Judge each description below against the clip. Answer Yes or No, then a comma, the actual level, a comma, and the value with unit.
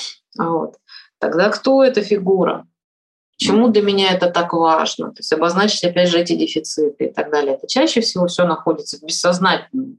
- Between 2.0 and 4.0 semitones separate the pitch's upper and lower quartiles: No, average, 4.6 semitones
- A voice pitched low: No, medium, 175 Hz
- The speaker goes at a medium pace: No, fast, 170 wpm